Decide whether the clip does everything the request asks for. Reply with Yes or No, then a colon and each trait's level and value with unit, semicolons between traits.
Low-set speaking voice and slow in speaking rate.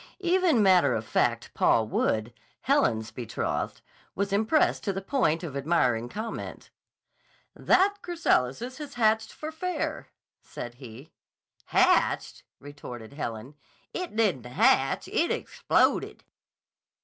No: medium, 180 Hz; slow, 115 wpm